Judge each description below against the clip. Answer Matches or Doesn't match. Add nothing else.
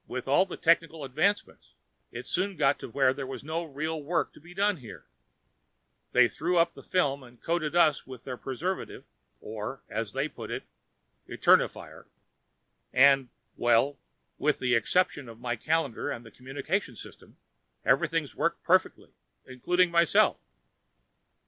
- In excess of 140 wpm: Matches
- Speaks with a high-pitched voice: Doesn't match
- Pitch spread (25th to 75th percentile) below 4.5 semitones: Doesn't match